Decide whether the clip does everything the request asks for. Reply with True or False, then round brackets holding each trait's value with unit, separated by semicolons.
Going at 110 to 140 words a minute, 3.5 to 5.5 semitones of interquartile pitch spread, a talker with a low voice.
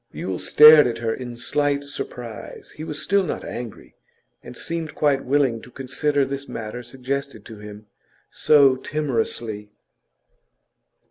True (135 wpm; 4.1 semitones; 130 Hz)